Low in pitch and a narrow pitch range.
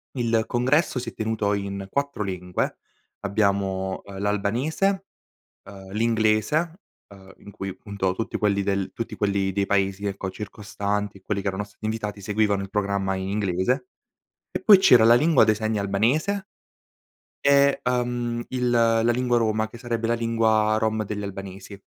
No: low, 105 Hz; average, 3.1 semitones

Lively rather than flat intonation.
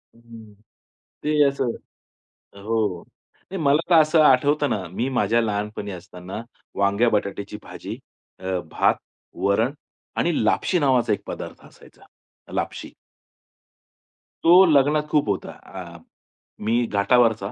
Yes: wide, 6.3 semitones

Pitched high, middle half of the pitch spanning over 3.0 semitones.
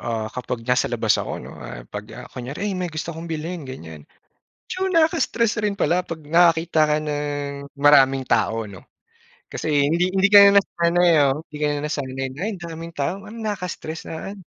No: medium, 160 Hz; average, 4.6 semitones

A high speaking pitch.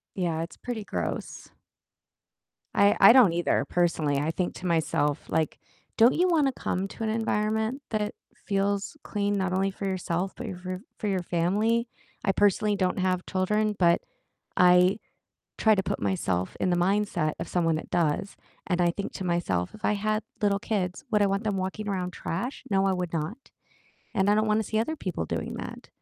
Yes: high, 195 Hz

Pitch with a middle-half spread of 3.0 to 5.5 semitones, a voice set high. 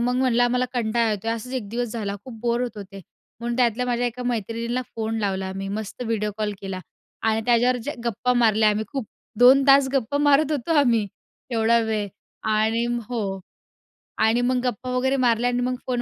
No: narrow, 2.4 semitones; high, 235 Hz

